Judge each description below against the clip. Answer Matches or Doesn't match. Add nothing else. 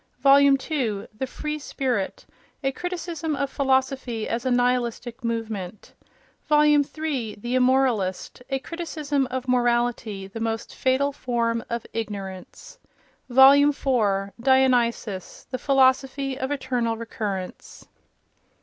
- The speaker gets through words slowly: Matches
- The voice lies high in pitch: Matches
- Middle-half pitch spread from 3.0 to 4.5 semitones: Matches